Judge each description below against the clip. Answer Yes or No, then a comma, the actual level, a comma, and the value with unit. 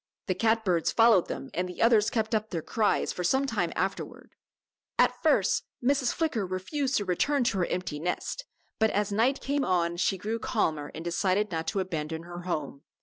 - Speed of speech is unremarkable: Yes, average, 195 wpm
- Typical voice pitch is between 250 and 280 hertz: No, high, 195 Hz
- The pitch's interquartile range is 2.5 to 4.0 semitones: No, average, 4.6 semitones